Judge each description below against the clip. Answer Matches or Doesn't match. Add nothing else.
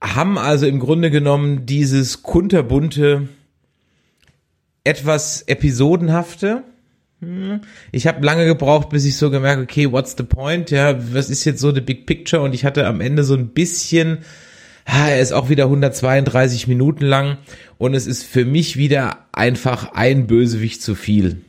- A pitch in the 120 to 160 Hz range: Matches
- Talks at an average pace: Matches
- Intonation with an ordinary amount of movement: Matches